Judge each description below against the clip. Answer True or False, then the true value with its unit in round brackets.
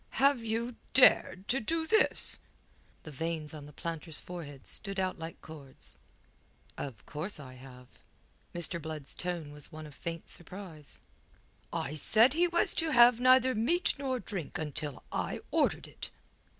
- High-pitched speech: False (175 Hz)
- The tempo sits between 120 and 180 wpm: True (150 wpm)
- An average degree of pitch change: False (8.0 semitones)